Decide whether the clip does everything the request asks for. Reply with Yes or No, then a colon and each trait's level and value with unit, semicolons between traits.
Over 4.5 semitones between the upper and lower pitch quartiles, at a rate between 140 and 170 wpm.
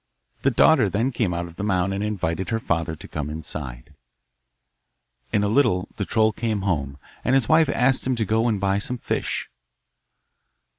No: average, 5.1 semitones; average, 185 wpm